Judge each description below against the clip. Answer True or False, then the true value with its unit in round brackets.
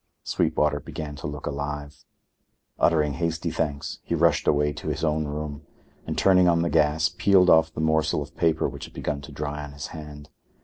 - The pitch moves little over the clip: True (2.0 semitones)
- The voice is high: False (75 Hz)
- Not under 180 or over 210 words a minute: True (190 wpm)